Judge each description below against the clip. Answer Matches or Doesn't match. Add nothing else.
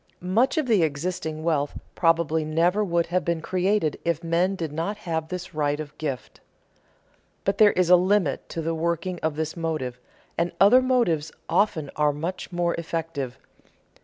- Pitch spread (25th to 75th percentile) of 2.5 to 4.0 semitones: Matches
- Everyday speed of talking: Matches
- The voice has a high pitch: Doesn't match